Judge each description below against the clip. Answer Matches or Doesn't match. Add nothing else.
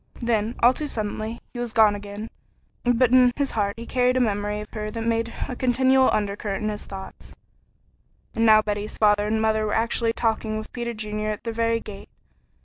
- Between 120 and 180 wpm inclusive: Doesn't match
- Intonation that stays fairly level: Matches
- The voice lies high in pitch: Matches